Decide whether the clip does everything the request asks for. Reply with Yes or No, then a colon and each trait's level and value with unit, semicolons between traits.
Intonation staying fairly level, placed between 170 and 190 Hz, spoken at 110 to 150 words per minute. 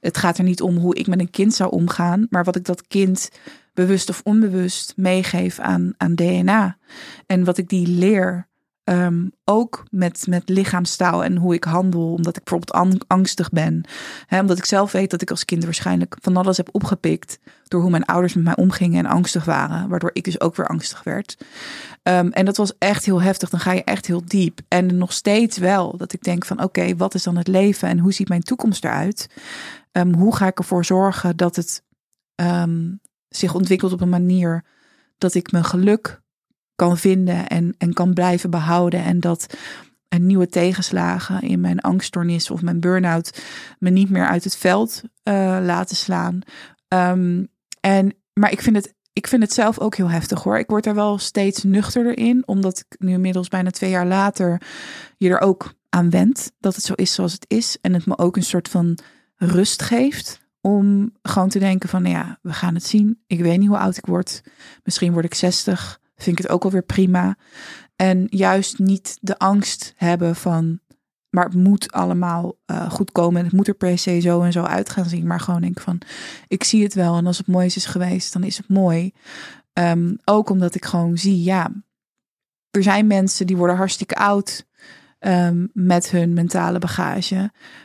No: narrow, 2.0 semitones; medium, 185 Hz; fast, 200 wpm